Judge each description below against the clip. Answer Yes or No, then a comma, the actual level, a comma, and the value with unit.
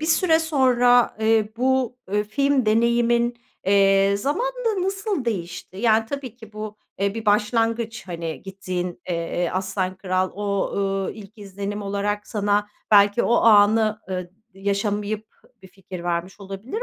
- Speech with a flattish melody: No, average, 3.4 semitones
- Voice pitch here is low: No, high, 210 Hz